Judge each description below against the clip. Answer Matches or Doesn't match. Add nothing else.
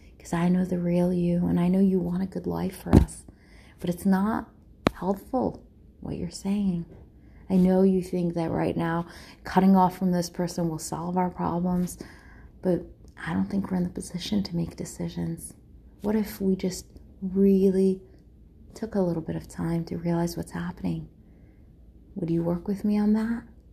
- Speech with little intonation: Matches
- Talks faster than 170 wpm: Matches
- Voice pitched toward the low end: Doesn't match